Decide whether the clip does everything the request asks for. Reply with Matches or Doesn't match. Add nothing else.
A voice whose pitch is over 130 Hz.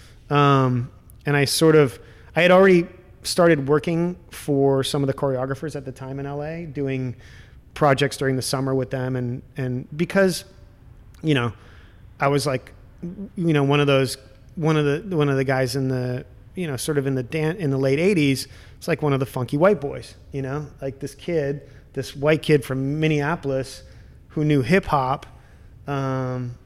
Matches